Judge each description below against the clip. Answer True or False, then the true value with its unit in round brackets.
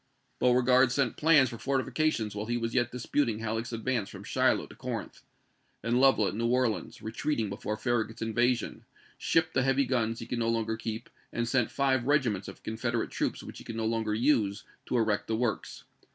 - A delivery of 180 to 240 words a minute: True (190 wpm)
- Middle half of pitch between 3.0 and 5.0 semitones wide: False (2.5 semitones)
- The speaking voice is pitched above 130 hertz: False (120 Hz)